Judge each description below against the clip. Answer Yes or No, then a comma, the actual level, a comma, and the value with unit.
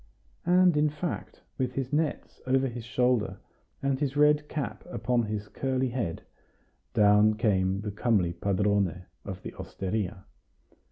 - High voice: No, low, 120 Hz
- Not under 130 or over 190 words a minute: Yes, slow, 135 wpm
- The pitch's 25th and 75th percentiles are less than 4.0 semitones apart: No, average, 5.0 semitones